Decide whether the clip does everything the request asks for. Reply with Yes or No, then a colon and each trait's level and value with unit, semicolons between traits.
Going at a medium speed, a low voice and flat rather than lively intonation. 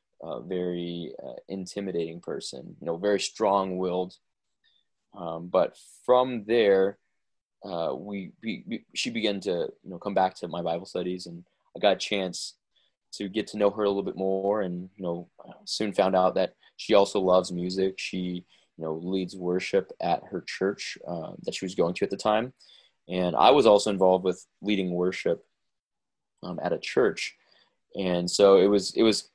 Yes: average, 180 wpm; very low, 95 Hz; narrow, 2.2 semitones